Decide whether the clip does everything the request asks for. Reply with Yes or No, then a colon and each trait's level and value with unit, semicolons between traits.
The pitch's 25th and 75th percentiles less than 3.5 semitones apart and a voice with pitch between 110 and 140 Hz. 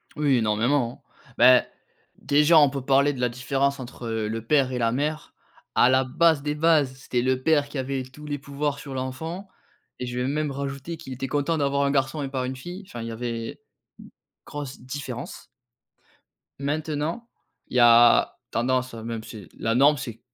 Yes: average, 2.8 semitones; low, 135 Hz